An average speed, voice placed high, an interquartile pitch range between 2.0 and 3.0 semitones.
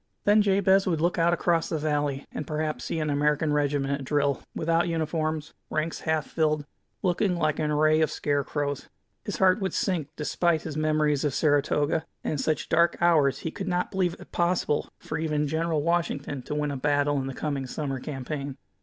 No: average, 190 wpm; medium, 155 Hz; narrow, 2.5 semitones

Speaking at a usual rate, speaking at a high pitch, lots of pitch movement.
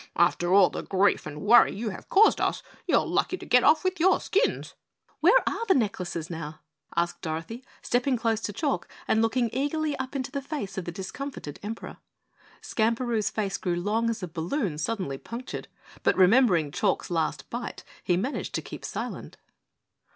Yes: average, 180 wpm; high, 220 Hz; wide, 6.9 semitones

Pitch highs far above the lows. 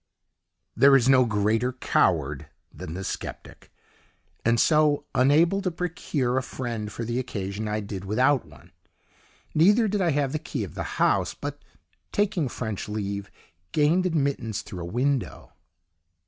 Yes: wide, 6.1 semitones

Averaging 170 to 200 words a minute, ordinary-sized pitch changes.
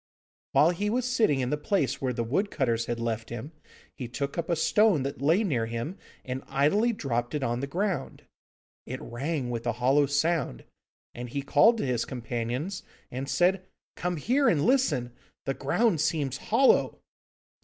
No: average, 175 wpm; wide, 6.4 semitones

